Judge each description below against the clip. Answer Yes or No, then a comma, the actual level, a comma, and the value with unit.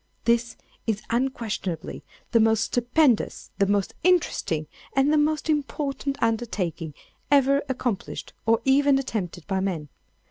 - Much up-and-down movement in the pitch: Yes, wide, 5.7 semitones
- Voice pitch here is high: Yes, high, 235 Hz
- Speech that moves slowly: Yes, slow, 120 wpm